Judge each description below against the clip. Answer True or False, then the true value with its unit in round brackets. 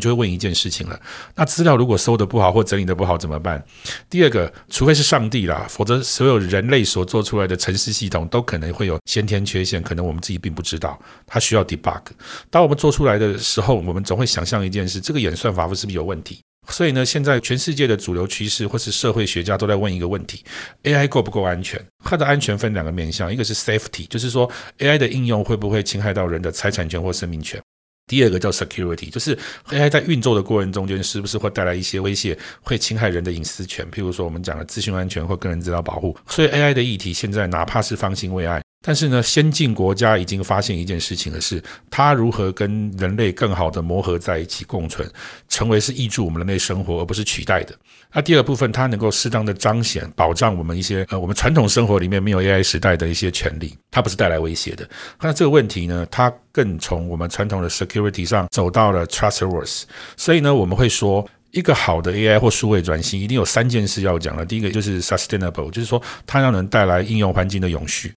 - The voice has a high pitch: False (100 Hz)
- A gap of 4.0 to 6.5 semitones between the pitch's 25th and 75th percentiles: True (4.5 semitones)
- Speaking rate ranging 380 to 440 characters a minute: True (395 characters per minute)